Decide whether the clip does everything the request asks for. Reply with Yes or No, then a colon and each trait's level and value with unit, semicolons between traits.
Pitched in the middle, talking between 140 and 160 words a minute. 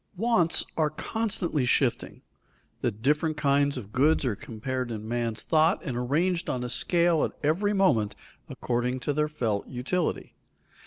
Yes: medium, 145 Hz; average, 145 wpm